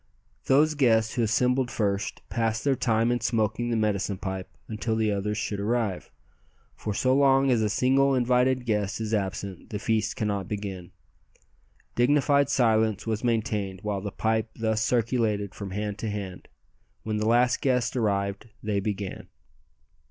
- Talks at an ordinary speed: Yes, average, 155 wpm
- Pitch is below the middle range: Yes, low, 110 Hz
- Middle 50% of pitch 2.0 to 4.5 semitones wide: Yes, average, 2.9 semitones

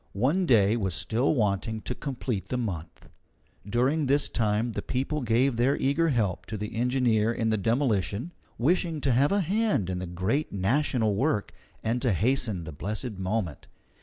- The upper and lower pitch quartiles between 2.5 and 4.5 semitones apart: No, average, 4.9 semitones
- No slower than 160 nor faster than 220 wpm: Yes, average, 170 wpm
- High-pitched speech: No, low, 115 Hz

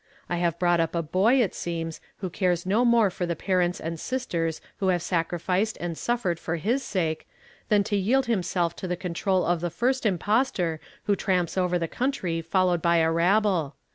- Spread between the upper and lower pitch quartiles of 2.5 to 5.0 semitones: Yes, average, 3.5 semitones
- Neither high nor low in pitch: Yes, medium, 180 Hz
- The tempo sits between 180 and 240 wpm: Yes, average, 200 wpm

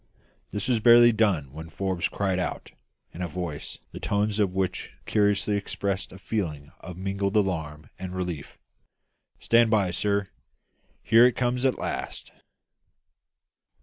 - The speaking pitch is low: Yes, low, 100 Hz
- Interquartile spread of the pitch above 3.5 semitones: No, average, 3.1 semitones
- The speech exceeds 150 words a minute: No, average, 140 wpm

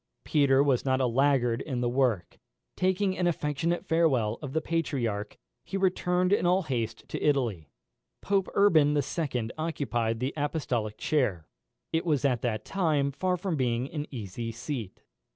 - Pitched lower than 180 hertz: Yes, medium, 140 Hz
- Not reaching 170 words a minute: Yes, average, 155 wpm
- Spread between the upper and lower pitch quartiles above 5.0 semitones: Yes, wide, 5.6 semitones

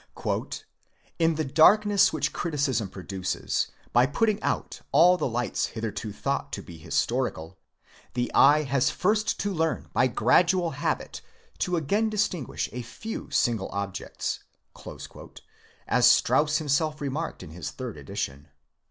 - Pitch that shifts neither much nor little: No, wide, 7.0 semitones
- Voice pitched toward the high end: No, medium, 140 Hz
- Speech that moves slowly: Yes, slow, 130 wpm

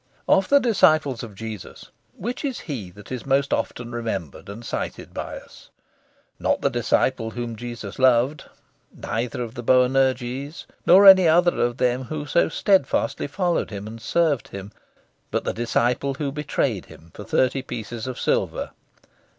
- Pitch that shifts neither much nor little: Yes, average, 4.5 semitones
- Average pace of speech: Yes, average, 160 wpm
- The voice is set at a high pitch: No, low, 125 Hz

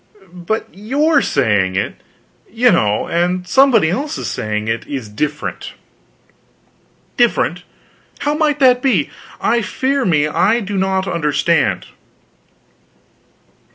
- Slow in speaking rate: Yes, slow, 110 wpm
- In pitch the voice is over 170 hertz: Yes, high, 190 Hz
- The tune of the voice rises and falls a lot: Yes, wide, 8.9 semitones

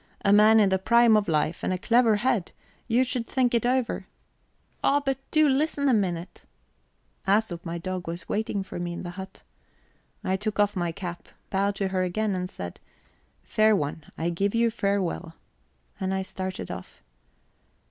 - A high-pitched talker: Yes, high, 200 Hz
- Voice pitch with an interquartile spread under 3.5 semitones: No, average, 4.1 semitones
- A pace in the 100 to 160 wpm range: No, average, 180 wpm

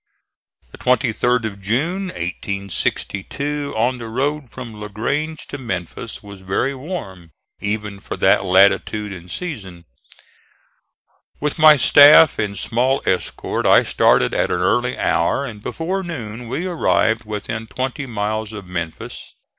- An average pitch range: No, wide, 5.8 semitones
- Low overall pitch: Yes, low, 115 Hz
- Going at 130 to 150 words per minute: Yes, slow, 135 wpm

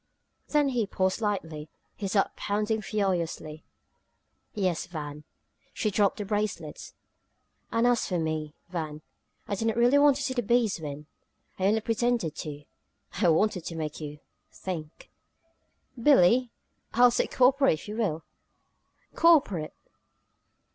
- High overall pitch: Yes, high, 200 Hz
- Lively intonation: Yes, wide, 6.6 semitones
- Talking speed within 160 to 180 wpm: No, slow, 135 wpm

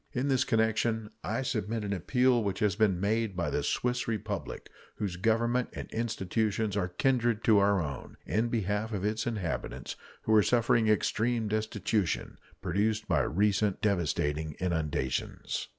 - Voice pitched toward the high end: No, low, 105 Hz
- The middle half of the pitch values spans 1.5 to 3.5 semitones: Yes, average, 2.8 semitones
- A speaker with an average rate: Yes, average, 150 wpm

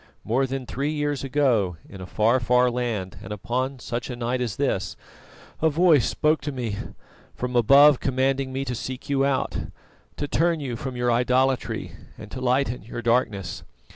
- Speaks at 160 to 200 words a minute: Yes, average, 175 wpm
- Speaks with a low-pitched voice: Yes, low, 125 Hz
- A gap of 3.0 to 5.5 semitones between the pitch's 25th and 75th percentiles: No, narrow, 2.5 semitones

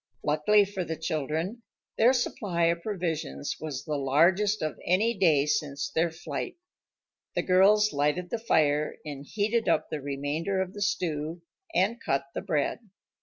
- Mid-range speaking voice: Yes, medium, 165 Hz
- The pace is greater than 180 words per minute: No, average, 155 wpm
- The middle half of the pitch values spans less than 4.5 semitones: No, average, 5.1 semitones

